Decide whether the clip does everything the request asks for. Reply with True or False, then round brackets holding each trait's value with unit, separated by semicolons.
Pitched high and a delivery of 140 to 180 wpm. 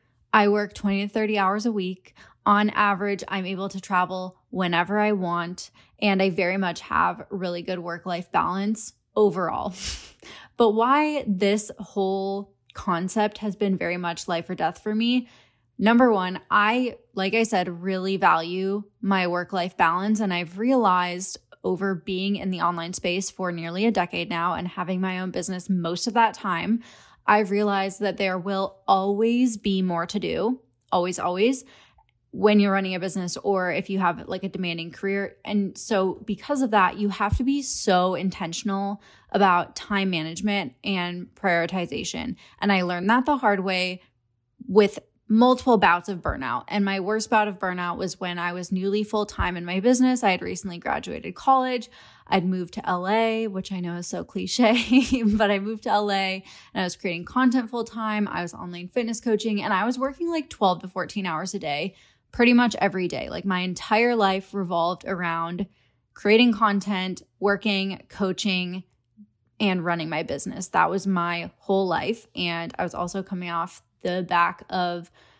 True (195 Hz; 175 wpm)